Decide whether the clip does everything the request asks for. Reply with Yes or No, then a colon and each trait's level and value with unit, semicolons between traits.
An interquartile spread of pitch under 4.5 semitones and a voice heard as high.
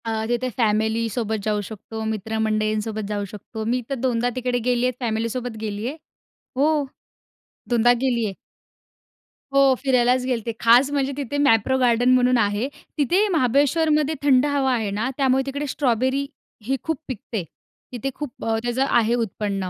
Yes: average, 3.3 semitones; high, 240 Hz